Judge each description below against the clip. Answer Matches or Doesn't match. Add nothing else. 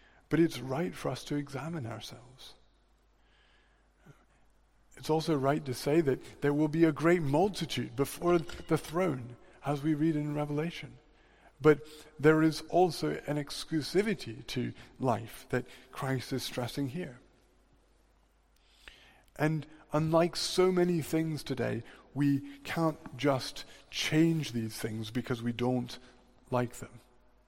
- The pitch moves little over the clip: Doesn't match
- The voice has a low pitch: Doesn't match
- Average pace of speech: Doesn't match